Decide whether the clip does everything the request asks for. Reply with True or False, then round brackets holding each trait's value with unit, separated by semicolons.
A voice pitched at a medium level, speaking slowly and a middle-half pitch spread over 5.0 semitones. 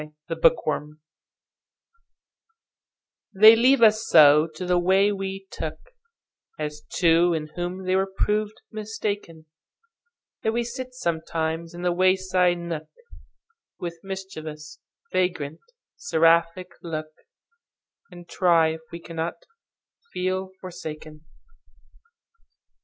False (180 Hz; 90 wpm; 4.0 semitones)